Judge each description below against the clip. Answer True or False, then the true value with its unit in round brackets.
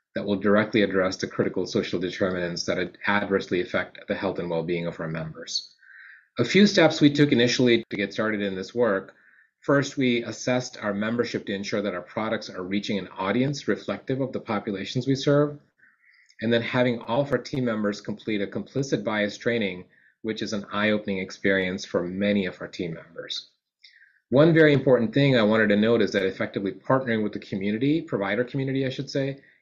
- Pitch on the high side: False (110 Hz)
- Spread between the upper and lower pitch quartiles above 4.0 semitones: True (4.7 semitones)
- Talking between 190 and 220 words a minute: True (195 wpm)